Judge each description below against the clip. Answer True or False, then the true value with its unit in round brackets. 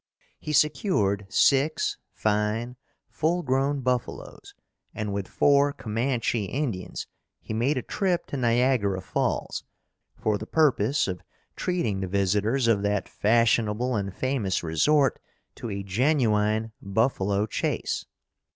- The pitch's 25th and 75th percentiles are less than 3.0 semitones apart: False (5.1 semitones)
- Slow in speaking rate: True (120 wpm)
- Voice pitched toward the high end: False (115 Hz)